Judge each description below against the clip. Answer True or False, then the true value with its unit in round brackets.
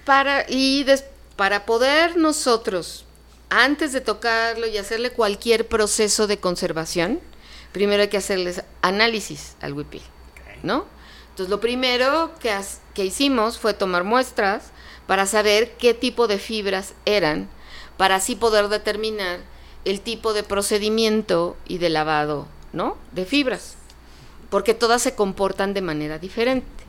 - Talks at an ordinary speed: True (135 wpm)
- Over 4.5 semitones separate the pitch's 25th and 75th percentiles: False (3.4 semitones)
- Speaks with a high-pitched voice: True (215 Hz)